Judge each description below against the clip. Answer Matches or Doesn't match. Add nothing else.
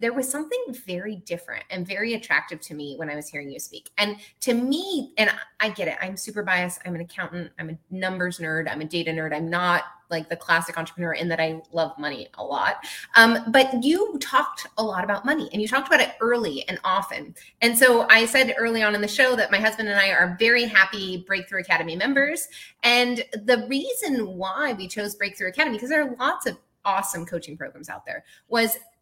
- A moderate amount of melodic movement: Doesn't match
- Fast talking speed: Matches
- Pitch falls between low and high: Doesn't match